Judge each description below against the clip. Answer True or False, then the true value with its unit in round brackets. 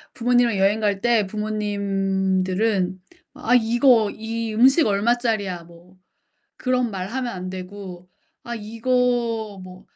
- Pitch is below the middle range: False (215 Hz)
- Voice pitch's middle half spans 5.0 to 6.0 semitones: False (3.6 semitones)